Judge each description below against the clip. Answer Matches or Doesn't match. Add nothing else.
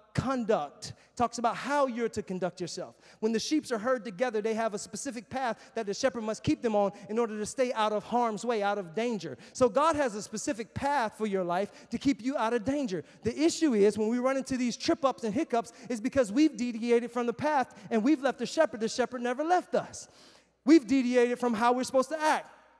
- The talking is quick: Matches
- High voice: Matches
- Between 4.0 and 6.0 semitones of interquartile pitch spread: Doesn't match